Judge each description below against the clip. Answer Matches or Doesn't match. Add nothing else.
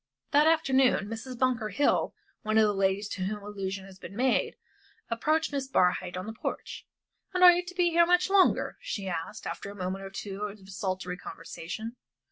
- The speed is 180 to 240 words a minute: Matches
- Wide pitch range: Matches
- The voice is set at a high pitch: Matches